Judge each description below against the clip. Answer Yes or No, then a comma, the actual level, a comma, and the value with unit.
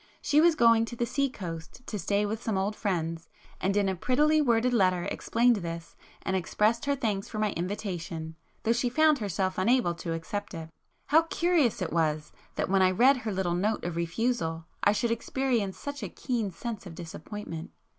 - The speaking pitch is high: Yes, high, 205 Hz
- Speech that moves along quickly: No, average, 195 wpm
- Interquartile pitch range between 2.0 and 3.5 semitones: No, wide, 5.5 semitones